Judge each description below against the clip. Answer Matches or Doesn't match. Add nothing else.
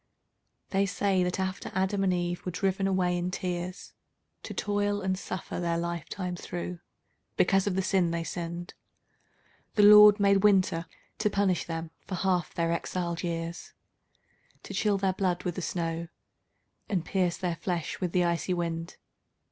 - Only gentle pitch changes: Matches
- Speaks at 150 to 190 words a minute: Matches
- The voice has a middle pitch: Matches